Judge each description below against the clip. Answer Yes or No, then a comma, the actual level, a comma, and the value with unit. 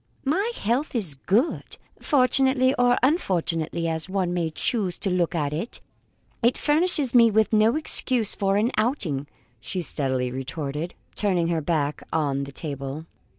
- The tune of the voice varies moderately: No, wide, 7.9 semitones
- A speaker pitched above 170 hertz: Yes, medium, 185 Hz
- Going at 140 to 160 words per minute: Yes, average, 150 wpm